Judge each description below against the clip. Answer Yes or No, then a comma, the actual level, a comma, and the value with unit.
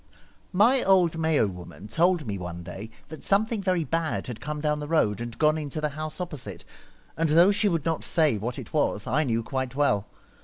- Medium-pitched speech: Yes, medium, 150 Hz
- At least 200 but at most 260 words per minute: Yes, fast, 205 wpm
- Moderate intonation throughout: No, wide, 5.9 semitones